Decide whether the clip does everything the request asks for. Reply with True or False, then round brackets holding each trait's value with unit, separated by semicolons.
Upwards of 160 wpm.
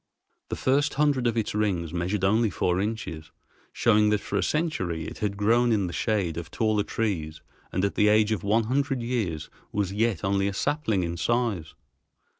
True (190 wpm)